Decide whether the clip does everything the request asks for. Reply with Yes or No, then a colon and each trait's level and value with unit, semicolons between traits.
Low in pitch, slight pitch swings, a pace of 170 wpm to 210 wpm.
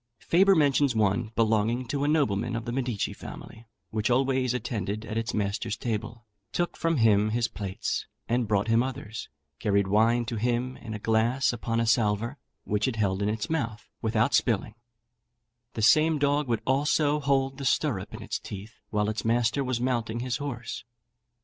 No: low, 115 Hz; average, 3.4 semitones; average, 175 wpm